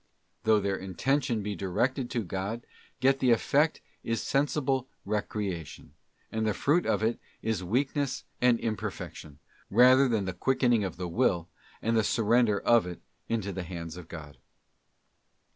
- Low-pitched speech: Yes, low, 110 Hz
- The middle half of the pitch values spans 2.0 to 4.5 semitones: No, average, 4.9 semitones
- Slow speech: No, average, 150 wpm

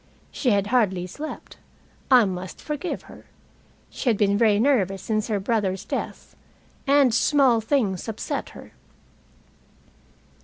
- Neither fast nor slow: No, slow, 125 wpm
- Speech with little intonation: No, average, 4.7 semitones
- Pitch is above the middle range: Yes, high, 220 Hz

